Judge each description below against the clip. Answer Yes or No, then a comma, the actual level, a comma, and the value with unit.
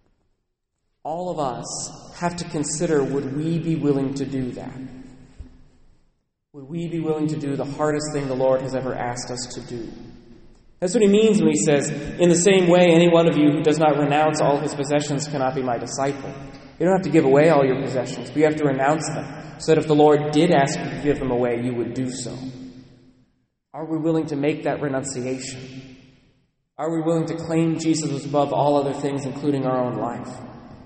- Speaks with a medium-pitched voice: Yes, medium, 145 Hz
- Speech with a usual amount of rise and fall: Yes, average, 3.0 semitones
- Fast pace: Yes, fast, 210 wpm